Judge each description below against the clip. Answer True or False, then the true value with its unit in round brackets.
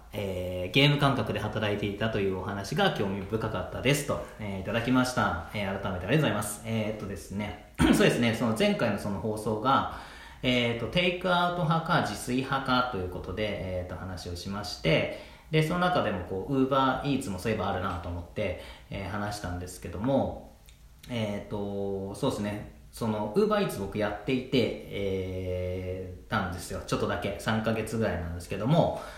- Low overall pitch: True (105 Hz)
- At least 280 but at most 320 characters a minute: False (395 characters per minute)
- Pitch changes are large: False (4.8 semitones)